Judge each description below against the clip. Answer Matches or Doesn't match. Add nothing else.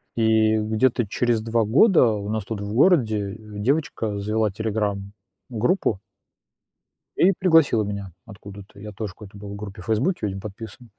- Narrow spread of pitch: Matches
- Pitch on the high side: Doesn't match